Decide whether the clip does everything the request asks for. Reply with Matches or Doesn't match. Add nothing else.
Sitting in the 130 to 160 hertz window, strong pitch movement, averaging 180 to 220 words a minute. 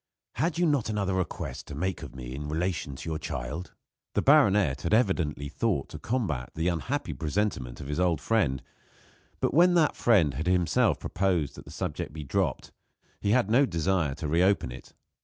Doesn't match